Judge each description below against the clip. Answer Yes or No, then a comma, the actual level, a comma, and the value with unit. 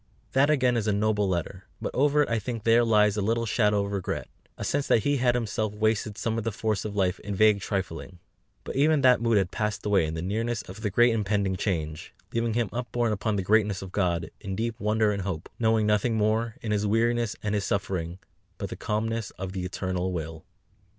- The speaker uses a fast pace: Yes, fast, 225 wpm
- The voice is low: Yes, low, 105 Hz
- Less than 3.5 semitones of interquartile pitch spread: Yes, average, 2.8 semitones